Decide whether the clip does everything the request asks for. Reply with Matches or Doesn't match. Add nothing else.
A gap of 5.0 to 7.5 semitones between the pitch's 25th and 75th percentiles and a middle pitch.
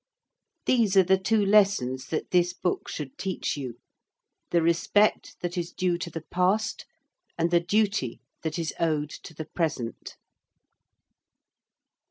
Doesn't match